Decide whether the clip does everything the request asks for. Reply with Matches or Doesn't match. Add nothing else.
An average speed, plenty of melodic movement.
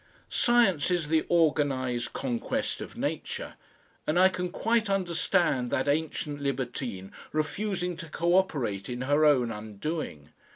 Doesn't match